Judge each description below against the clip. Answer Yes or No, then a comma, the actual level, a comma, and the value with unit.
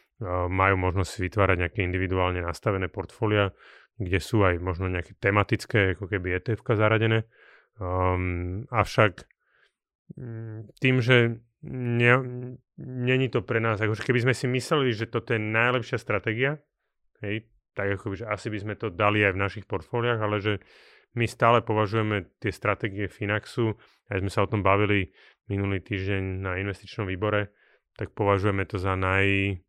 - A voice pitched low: Yes, low, 105 Hz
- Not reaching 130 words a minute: No, average, 150 wpm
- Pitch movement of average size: Yes, average, 3.2 semitones